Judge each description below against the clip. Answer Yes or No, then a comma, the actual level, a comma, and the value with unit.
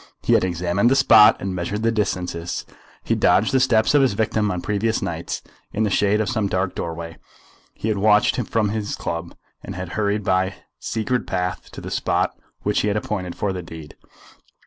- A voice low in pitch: Yes, low, 100 Hz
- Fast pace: Yes, fast, 210 wpm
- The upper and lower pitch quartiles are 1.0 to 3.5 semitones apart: Yes, average, 3.2 semitones